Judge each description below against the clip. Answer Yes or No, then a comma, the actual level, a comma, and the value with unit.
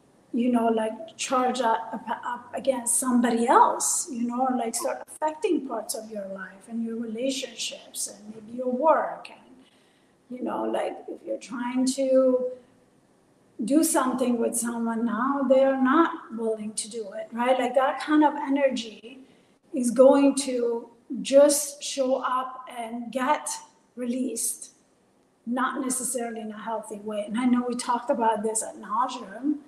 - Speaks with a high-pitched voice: Yes, very high, 250 Hz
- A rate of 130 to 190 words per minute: Yes, average, 150 wpm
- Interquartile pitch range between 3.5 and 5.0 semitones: No, average, 2.7 semitones